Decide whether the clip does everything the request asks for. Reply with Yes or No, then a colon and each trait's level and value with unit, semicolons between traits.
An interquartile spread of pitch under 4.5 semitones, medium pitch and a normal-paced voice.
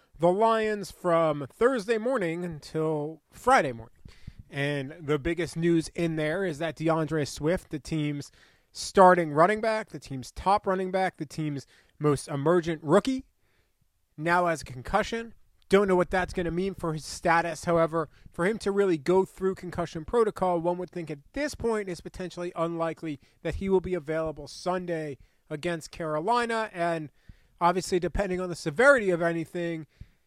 Yes: average, 3.1 semitones; medium, 170 Hz; average, 160 wpm